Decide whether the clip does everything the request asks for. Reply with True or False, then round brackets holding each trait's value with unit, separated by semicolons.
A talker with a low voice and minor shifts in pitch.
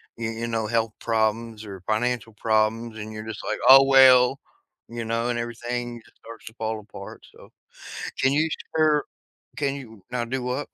True (115 Hz; 2.1 semitones)